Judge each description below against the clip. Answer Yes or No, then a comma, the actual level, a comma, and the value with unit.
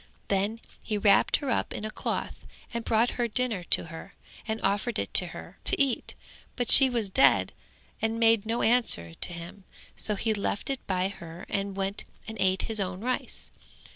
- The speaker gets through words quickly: No, average, 185 wpm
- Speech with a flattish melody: No, average, 3.2 semitones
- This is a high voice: Yes, high, 215 Hz